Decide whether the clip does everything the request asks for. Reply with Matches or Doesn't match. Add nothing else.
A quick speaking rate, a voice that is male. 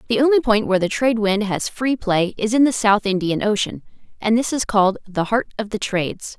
Doesn't match